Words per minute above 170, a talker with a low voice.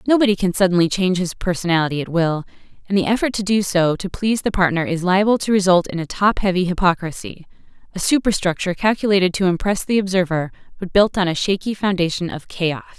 No: average, 185 wpm; medium, 185 Hz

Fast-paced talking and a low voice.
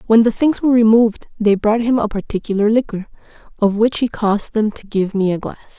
No: fast, 220 wpm; high, 220 Hz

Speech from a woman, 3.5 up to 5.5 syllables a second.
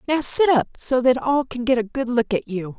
Yes: female; 5.1 syllables/s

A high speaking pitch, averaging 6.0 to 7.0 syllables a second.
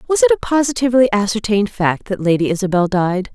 Yes: high, 220 Hz; 6.5 syllables/s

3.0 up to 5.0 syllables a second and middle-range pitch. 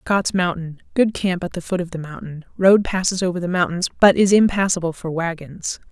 No: 5.3 syllables/s; medium, 180 Hz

